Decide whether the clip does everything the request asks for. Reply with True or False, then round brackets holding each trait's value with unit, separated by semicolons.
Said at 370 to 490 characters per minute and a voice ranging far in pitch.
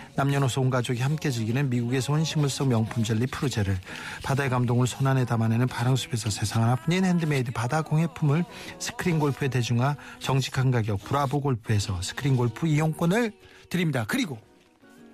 False (400 characters per minute; 3.4 semitones)